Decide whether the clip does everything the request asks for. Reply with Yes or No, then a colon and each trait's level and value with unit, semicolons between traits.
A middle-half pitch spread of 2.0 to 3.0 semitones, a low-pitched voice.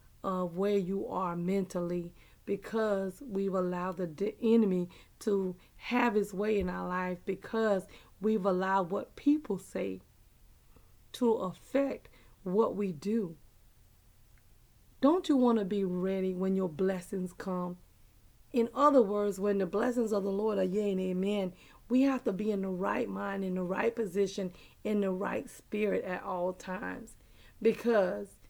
No: average, 2.7 semitones; high, 195 Hz